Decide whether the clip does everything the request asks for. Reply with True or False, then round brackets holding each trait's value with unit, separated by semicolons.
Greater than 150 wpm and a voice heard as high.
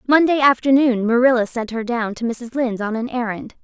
True (200 wpm; 240 Hz)